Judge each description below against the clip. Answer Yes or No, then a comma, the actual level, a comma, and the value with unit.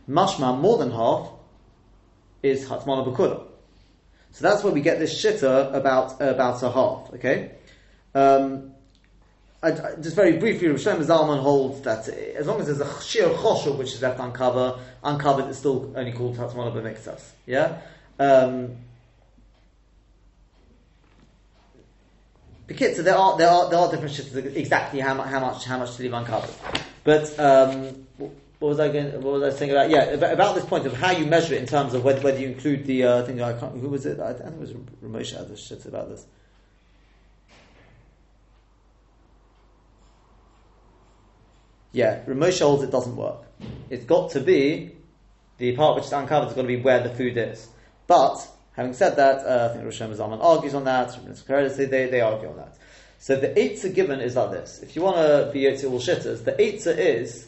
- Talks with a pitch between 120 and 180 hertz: Yes, low, 135 Hz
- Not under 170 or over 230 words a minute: Yes, average, 180 wpm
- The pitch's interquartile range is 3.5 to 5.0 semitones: No, average, 2.8 semitones